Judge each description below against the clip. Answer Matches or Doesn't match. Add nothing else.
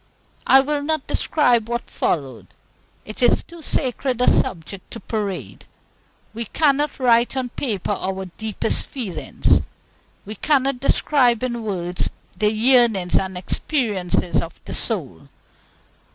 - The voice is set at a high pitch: Matches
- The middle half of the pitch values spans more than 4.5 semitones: Matches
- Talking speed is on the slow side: Matches